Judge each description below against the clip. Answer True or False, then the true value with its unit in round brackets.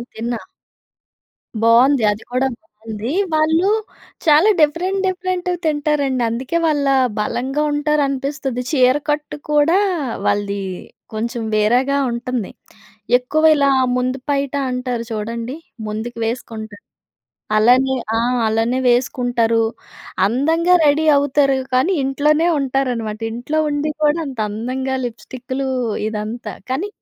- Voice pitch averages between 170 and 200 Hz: False (260 Hz)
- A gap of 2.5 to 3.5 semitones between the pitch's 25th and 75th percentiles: False (4.1 semitones)